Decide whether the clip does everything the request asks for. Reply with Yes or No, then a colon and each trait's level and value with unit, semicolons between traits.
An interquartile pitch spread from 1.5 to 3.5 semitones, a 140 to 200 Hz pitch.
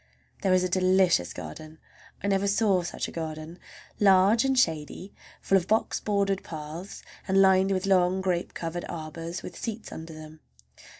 Yes: average, 3.1 semitones; medium, 185 Hz